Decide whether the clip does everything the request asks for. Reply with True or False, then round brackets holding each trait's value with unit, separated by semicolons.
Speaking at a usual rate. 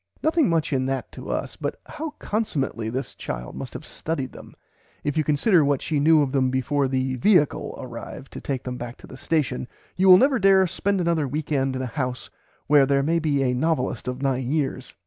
False (220 wpm)